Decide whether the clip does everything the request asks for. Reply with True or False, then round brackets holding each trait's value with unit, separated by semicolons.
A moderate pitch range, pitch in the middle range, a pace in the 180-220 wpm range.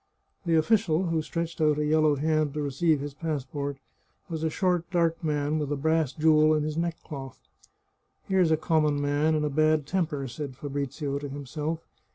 False (1.9 semitones; 155 Hz; 185 wpm)